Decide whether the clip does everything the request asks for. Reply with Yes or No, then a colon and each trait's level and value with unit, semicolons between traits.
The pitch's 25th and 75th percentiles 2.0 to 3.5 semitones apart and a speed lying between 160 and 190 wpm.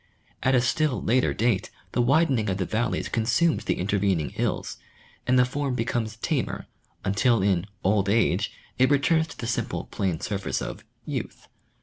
No: average, 4.5 semitones; average, 180 wpm